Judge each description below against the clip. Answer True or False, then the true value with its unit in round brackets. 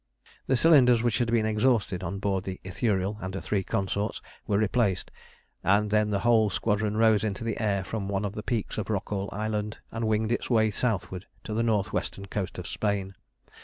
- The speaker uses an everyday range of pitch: False (2.2 semitones)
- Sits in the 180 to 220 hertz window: False (105 Hz)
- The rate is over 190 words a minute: True (200 wpm)